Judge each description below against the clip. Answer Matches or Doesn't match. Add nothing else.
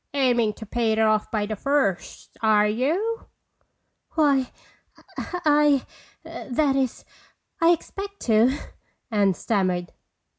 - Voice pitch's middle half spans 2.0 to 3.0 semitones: Doesn't match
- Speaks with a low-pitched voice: Doesn't match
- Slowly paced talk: Matches